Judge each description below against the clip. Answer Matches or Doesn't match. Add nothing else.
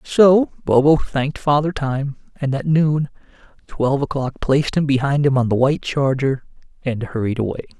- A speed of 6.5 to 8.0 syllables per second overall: Doesn't match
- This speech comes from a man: Matches